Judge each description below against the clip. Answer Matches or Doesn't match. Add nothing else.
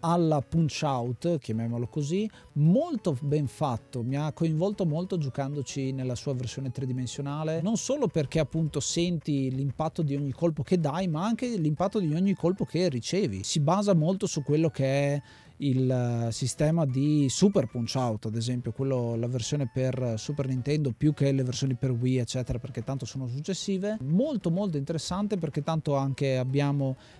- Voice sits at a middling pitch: Matches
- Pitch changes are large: Doesn't match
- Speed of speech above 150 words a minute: Matches